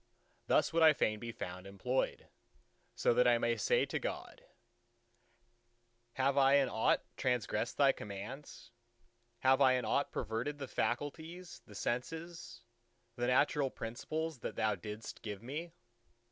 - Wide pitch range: No, average, 4.2 semitones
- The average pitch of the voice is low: Yes, low, 125 Hz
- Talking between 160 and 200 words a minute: No, average, 145 wpm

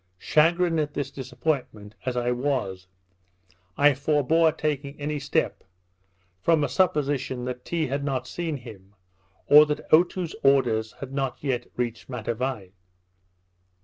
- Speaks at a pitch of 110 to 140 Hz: Yes, low, 135 Hz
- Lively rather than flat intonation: No, average, 3.5 semitones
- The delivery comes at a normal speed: No, slow, 130 wpm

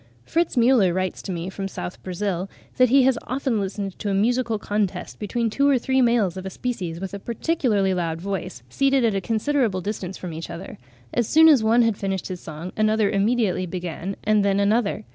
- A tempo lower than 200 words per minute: No, fast, 205 wpm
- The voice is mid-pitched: No, high, 205 Hz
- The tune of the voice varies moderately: Yes, average, 4.2 semitones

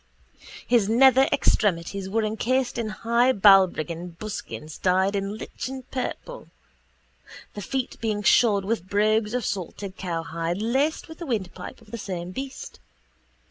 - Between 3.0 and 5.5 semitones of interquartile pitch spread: Yes, average, 4.3 semitones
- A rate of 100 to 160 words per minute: Yes, slow, 135 wpm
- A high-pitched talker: Yes, high, 210 Hz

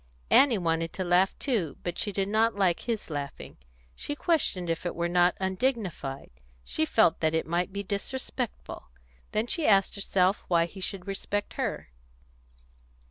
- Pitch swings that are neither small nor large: Yes, average, 3.7 semitones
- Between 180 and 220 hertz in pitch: Yes, high, 190 Hz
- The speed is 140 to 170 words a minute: Yes, average, 160 wpm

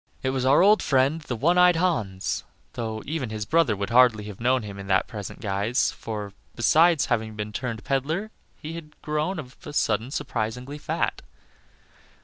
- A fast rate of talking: No, average, 170 wpm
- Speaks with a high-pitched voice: No, low, 125 Hz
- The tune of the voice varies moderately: No, wide, 5.8 semitones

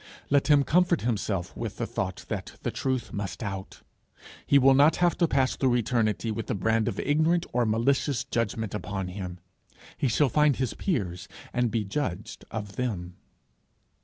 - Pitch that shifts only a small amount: No, average, 5.3 semitones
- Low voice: Yes, low, 120 Hz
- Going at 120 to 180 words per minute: Yes, average, 170 wpm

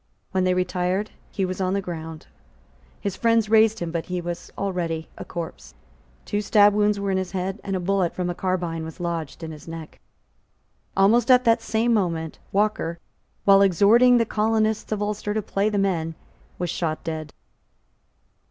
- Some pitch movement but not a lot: Yes, average, 3.5 semitones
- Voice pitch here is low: No, high, 190 Hz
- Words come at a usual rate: Yes, average, 180 wpm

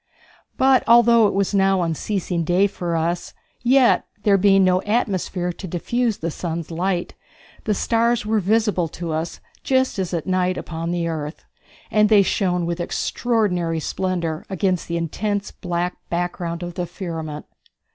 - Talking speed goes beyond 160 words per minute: No, average, 155 wpm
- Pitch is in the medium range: Yes, medium, 180 Hz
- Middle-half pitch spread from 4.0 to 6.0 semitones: No, average, 3.4 semitones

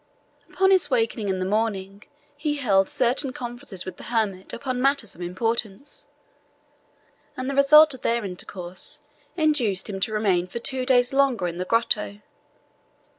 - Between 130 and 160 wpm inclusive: Yes, average, 155 wpm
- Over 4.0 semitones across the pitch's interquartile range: Yes, wide, 5.5 semitones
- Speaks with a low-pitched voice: No, high, 230 Hz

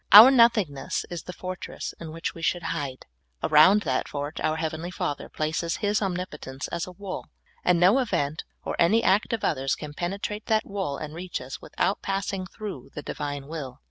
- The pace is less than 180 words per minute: No, average, 185 wpm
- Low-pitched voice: No, medium, 170 Hz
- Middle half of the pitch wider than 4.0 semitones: Yes, average, 4.7 semitones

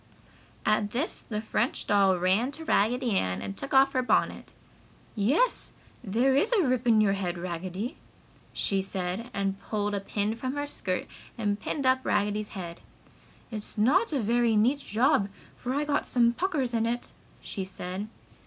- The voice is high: Yes, high, 220 Hz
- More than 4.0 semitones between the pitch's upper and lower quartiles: Yes, average, 4.7 semitones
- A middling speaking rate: Yes, average, 170 wpm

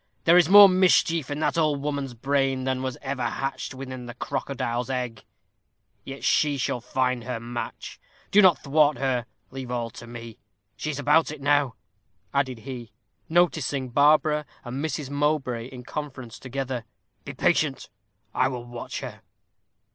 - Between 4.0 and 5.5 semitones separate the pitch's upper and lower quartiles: No, average, 3.1 semitones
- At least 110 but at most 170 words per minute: Yes, average, 155 wpm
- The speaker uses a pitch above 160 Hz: No, low, 135 Hz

